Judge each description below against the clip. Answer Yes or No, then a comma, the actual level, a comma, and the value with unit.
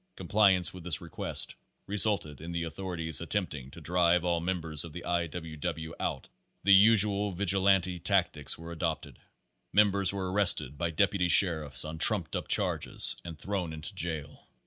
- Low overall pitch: Yes, very low, 85 Hz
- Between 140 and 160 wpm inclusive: No, average, 170 wpm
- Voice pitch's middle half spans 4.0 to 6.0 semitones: No, average, 3.2 semitones